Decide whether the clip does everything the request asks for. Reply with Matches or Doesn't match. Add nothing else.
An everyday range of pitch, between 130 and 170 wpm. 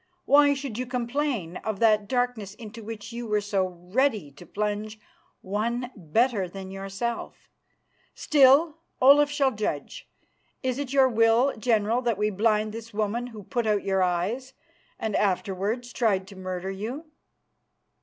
Matches